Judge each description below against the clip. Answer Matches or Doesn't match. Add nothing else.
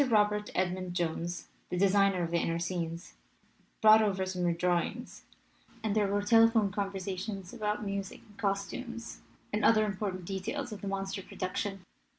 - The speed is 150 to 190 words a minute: Matches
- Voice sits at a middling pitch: Doesn't match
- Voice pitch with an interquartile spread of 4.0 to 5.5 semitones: Doesn't match